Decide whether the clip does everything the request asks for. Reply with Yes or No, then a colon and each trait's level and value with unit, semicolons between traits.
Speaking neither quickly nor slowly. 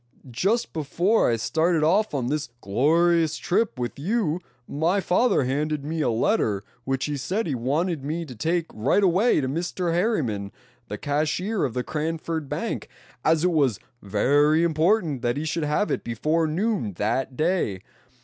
Yes: average, 165 wpm